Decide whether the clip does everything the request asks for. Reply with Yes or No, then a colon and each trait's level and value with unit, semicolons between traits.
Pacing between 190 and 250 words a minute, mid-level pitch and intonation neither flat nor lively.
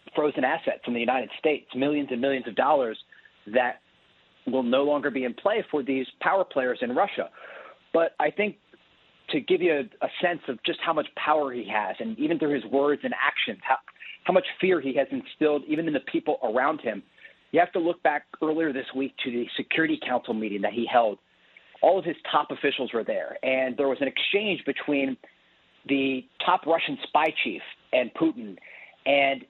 Yes: average, 195 wpm; medium, 145 Hz; average, 4.0 semitones